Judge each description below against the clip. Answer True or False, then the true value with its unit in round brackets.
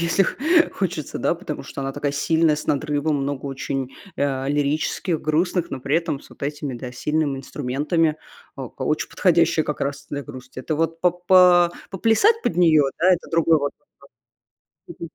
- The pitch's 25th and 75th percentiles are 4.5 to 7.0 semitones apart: False (3.2 semitones)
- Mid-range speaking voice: True (150 Hz)